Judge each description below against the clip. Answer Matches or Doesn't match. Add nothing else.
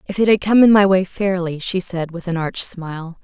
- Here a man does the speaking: Doesn't match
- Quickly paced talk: Matches